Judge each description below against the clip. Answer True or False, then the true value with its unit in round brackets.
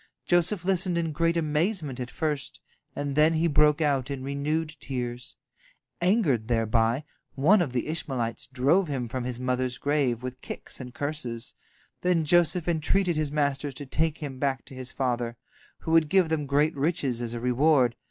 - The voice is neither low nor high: True (145 Hz)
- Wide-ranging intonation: False (4.1 semitones)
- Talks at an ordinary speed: True (170 wpm)